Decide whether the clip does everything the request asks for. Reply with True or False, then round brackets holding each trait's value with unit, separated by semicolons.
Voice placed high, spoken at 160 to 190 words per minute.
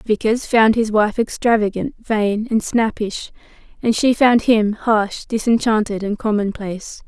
False (220 Hz; 135 wpm)